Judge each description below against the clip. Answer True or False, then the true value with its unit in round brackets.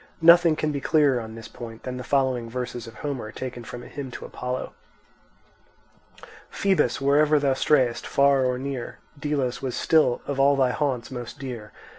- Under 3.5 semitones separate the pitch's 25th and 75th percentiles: True (2.7 semitones)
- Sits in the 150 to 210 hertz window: False (130 Hz)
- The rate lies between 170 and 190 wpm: True (175 wpm)